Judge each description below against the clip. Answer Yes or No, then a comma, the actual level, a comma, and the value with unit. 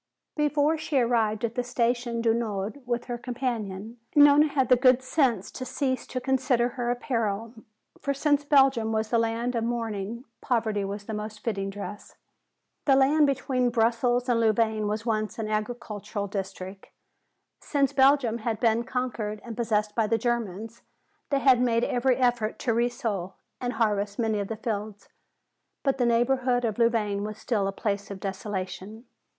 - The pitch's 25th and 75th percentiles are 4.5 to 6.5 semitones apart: No, average, 2.9 semitones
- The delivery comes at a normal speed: Yes, average, 165 wpm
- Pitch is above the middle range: Yes, high, 230 Hz